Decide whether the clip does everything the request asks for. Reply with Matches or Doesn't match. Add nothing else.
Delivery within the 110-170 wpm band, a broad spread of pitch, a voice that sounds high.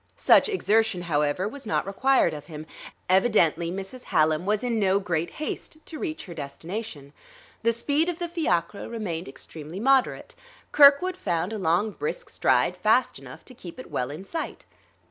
Matches